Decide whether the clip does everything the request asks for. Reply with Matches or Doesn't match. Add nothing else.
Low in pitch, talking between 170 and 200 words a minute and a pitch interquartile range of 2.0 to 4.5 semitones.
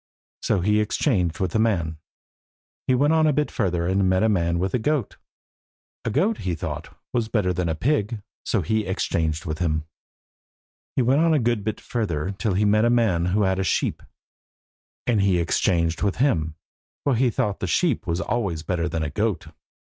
Doesn't match